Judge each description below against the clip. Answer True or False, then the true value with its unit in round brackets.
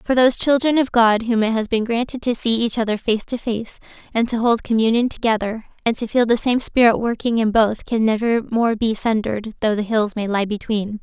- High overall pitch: True (225 Hz)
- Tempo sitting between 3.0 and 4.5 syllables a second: False (5.5 syllables/s)